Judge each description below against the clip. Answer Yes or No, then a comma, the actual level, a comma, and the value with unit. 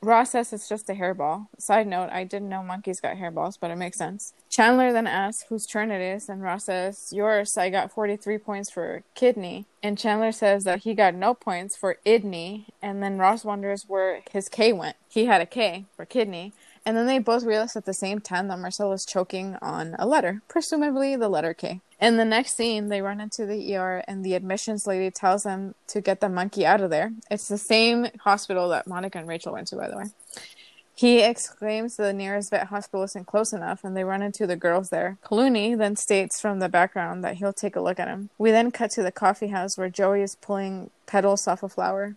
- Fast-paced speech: Yes, fast, 225 wpm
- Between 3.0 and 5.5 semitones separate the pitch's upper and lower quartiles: No, narrow, 2.6 semitones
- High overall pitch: Yes, high, 200 Hz